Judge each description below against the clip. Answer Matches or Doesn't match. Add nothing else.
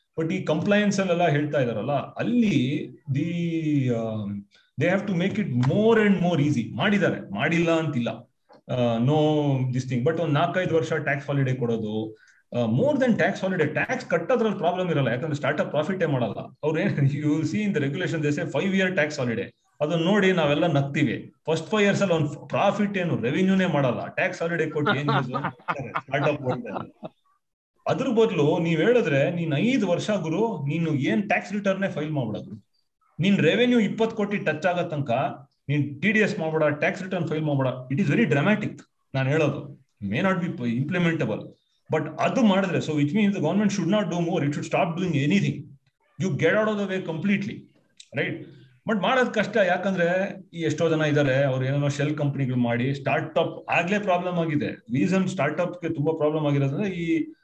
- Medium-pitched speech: Matches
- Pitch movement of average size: Matches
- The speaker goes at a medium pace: Doesn't match